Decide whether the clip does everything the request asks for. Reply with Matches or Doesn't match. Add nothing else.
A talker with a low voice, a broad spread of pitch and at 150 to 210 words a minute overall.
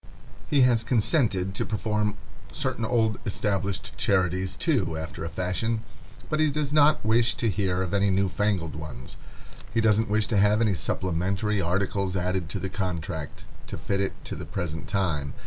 Doesn't match